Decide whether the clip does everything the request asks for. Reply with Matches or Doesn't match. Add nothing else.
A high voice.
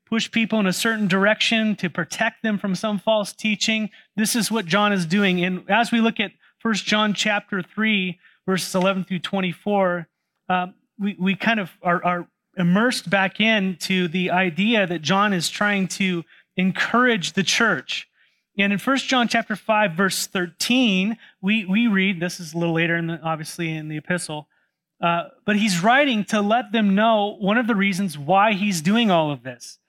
Matches